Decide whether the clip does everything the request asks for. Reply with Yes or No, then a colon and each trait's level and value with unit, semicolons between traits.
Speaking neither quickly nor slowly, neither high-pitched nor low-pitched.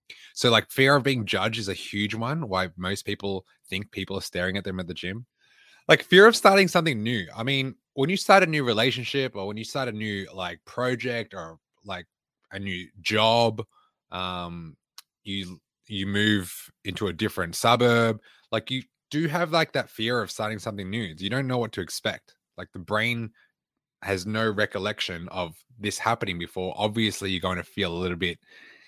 No: average, 190 wpm; low, 105 Hz